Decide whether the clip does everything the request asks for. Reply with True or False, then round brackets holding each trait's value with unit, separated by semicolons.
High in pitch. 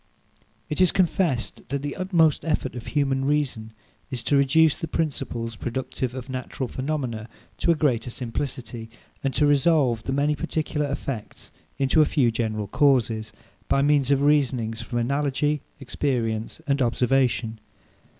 False (135 Hz)